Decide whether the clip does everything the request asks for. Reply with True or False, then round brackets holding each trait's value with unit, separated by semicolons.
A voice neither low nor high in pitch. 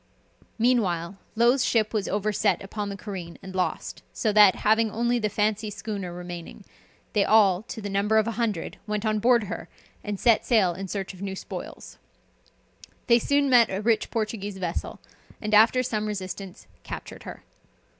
False (210 Hz)